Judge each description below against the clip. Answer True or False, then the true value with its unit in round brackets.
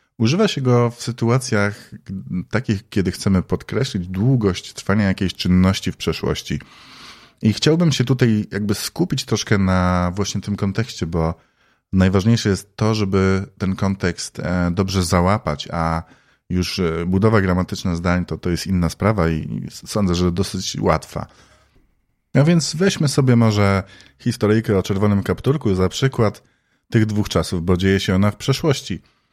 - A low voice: True (100 Hz)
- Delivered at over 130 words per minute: True (145 wpm)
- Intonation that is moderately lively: True (3.5 semitones)